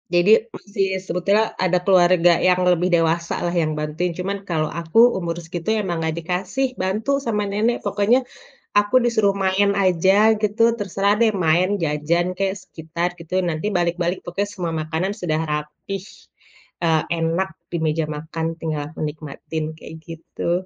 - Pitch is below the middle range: No, medium, 180 Hz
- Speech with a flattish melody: No, average, 3.5 semitones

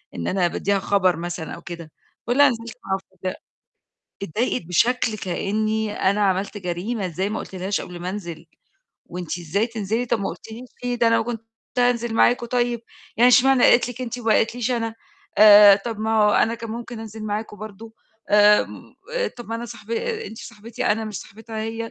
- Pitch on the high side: Yes, high, 220 Hz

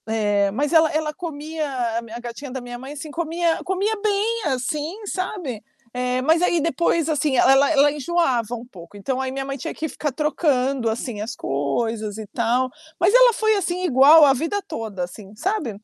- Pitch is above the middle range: Yes, very high, 275 Hz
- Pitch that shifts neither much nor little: No, wide, 5.7 semitones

